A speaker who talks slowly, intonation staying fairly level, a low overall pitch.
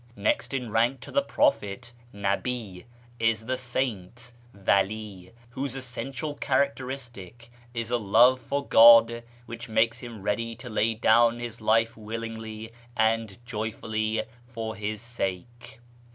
Yes: slow, 125 wpm; narrow, 2.0 semitones; low, 115 Hz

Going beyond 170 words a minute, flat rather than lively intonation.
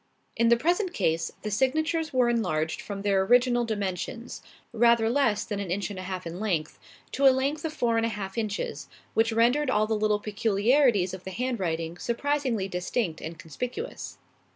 No: average, 180 wpm; average, 4.6 semitones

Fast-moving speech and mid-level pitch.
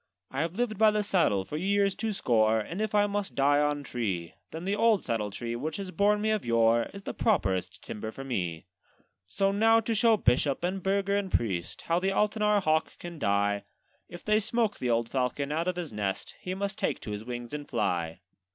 Yes: fast, 215 wpm; medium, 165 Hz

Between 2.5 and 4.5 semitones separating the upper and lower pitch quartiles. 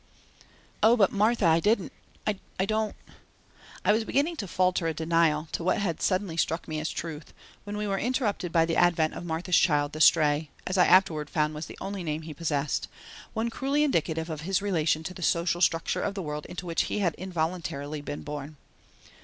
Yes: average, 4.0 semitones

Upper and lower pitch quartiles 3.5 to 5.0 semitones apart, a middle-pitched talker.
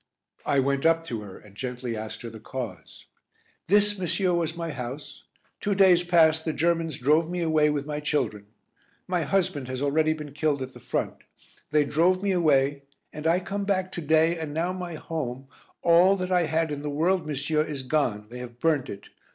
Yes: average, 4.1 semitones; medium, 155 Hz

